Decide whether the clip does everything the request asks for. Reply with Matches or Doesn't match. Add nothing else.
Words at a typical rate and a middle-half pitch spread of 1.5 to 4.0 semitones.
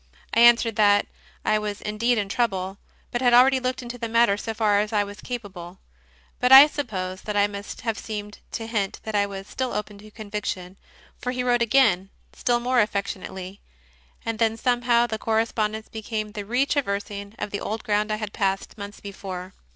Matches